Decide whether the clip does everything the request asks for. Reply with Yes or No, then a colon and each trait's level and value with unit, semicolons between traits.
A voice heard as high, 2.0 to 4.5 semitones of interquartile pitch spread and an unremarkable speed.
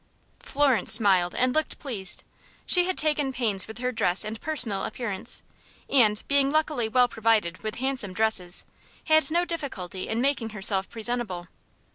No: high, 230 Hz; average, 5.3 semitones; average, 150 wpm